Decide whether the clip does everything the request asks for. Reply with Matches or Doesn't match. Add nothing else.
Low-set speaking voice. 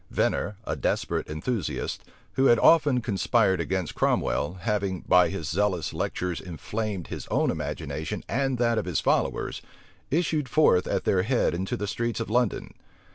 Matches